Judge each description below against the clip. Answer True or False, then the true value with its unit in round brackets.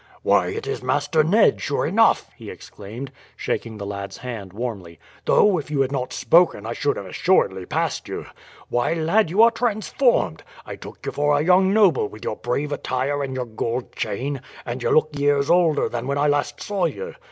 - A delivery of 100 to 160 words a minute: False (200 wpm)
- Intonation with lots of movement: True (6.7 semitones)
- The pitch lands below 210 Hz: True (140 Hz)